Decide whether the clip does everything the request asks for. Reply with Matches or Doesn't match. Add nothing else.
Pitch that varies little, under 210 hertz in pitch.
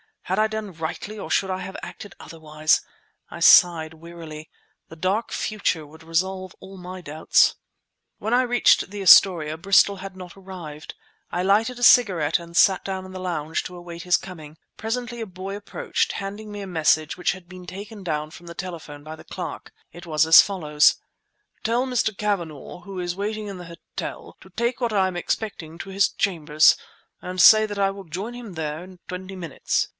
Doesn't match